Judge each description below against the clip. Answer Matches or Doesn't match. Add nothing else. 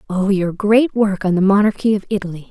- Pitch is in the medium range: Doesn't match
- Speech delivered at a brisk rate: Matches